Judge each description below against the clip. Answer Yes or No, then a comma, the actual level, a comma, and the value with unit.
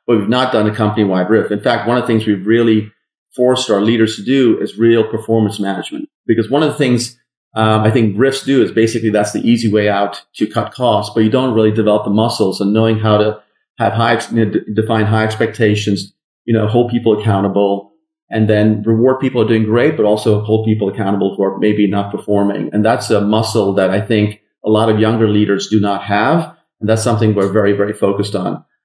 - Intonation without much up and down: Yes, narrow, 1.7 semitones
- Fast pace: Yes, fast, 225 wpm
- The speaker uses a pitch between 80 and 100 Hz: No, low, 110 Hz